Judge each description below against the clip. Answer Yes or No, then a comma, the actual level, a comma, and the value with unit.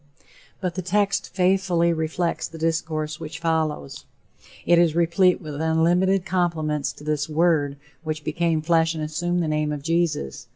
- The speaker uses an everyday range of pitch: No, narrow, 2.2 semitones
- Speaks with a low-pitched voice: No, medium, 165 Hz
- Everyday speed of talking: Yes, average, 155 wpm